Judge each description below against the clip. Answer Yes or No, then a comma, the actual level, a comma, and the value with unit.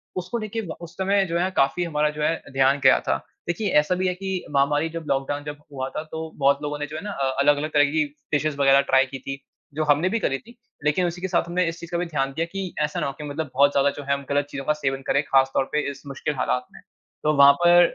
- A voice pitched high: No, medium, 150 Hz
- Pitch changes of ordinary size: Yes, average, 3.7 semitones